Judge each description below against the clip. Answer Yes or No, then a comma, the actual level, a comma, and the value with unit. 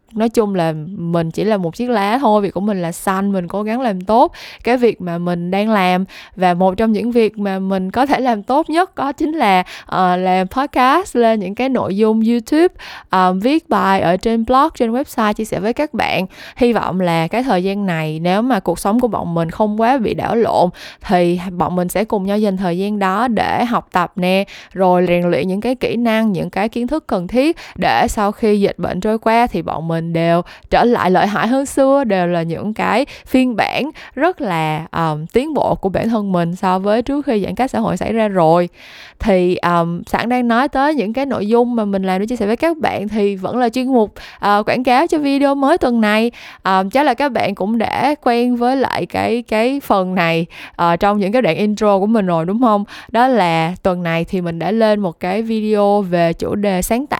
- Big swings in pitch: No, average, 4.7 semitones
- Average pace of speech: Yes, average, 240 wpm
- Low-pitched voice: No, high, 210 Hz